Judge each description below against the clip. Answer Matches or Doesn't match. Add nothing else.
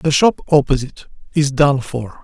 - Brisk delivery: Doesn't match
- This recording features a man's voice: Matches